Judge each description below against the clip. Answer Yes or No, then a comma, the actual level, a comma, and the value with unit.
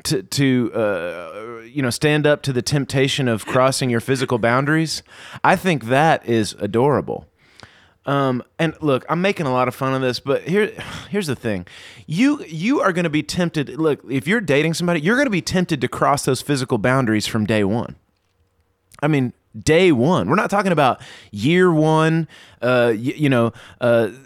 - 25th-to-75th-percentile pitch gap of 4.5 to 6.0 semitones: Yes, average, 5.2 semitones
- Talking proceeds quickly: No, average, 190 wpm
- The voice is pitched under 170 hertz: Yes, low, 135 Hz